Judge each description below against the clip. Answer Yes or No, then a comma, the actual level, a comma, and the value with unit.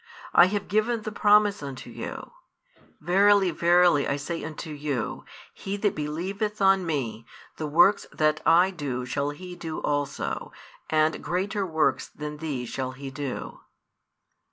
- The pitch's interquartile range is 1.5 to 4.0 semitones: No, average, 4.9 semitones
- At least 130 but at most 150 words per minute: Yes, average, 145 wpm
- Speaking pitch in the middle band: Yes, medium, 160 Hz